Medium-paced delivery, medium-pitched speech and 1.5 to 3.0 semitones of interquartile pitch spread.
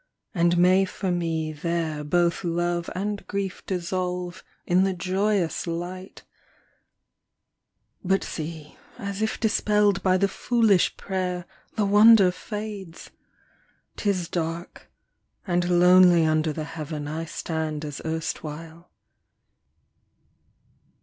No: slow, 105 wpm; medium, 180 Hz; average, 2.7 semitones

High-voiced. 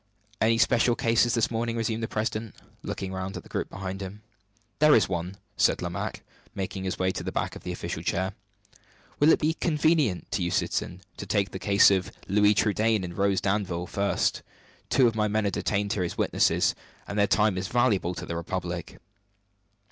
No: low, 100 Hz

